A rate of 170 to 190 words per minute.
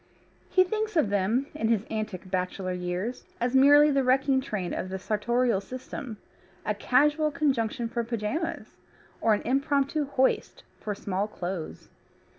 No: average, 145 wpm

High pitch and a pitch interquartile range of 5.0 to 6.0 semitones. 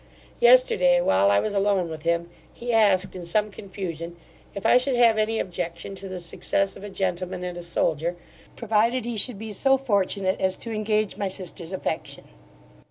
No: high, 195 Hz; average, 3.9 semitones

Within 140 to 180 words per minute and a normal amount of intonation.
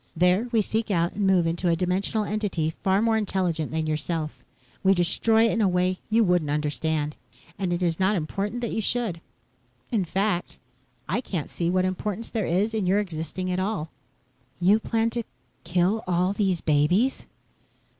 Yes: average, 175 wpm; average, 3.9 semitones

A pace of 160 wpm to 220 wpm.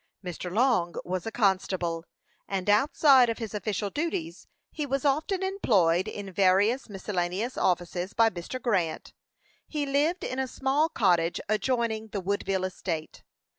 No: average, 140 wpm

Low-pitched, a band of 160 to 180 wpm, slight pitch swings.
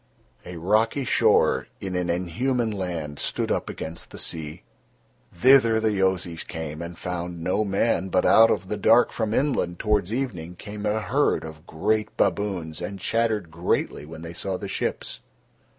No: very low, 95 Hz; average, 165 wpm; average, 4.4 semitones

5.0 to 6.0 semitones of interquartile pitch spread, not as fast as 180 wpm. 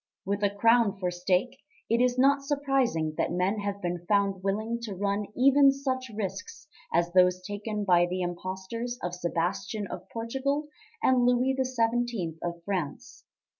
Yes: average, 5.3 semitones; average, 155 wpm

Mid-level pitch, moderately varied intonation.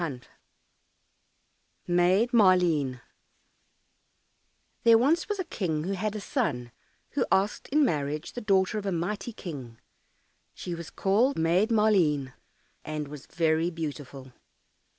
No: medium, 175 Hz; wide, 5.9 semitones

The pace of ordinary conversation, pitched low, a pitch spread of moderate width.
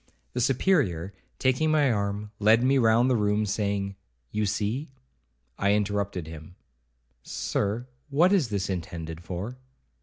No: slow, 125 wpm; low, 105 Hz; average, 5.0 semitones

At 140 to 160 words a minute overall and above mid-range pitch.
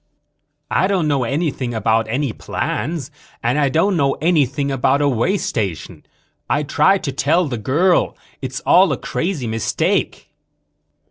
No: average, 145 wpm; medium, 140 Hz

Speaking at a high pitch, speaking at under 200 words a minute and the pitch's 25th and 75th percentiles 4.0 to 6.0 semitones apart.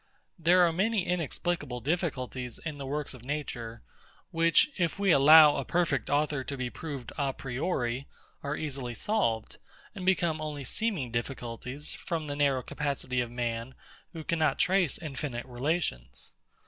No: medium, 145 Hz; average, 150 wpm; average, 4.7 semitones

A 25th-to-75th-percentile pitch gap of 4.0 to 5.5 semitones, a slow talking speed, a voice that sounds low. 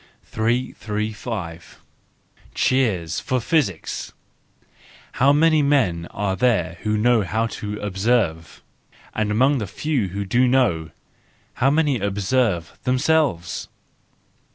Yes: average, 5.2 semitones; slow, 100 wpm; low, 110 Hz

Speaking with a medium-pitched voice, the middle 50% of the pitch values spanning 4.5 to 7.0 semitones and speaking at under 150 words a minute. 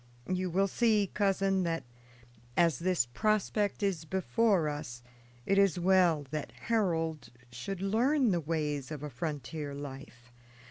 Yes: medium, 170 Hz; average, 4.9 semitones; slow, 135 wpm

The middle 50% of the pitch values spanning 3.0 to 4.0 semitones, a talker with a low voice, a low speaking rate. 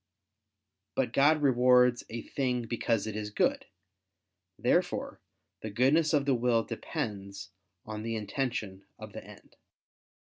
Yes: average, 3.3 semitones; low, 120 Hz; slow, 130 wpm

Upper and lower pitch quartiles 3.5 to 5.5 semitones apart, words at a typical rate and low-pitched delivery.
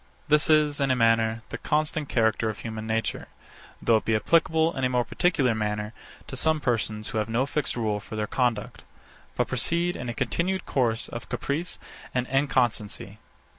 Yes: average, 5.1 semitones; average, 180 wpm; low, 120 Hz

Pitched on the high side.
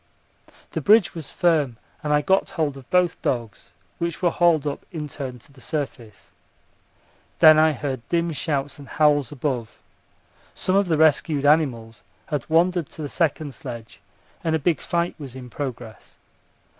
No: medium, 150 Hz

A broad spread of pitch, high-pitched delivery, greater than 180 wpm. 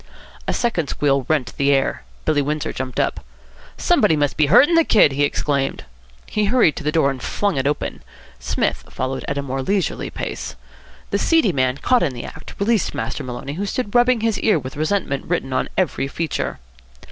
No: wide, 6.8 semitones; medium, 150 Hz; average, 195 wpm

